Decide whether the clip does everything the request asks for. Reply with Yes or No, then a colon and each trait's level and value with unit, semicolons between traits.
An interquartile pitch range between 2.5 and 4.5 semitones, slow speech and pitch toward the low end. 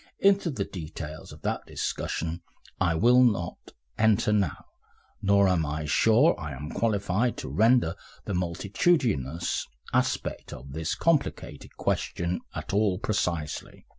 No: wide, 5.6 semitones; slow, 130 wpm; very low, 95 Hz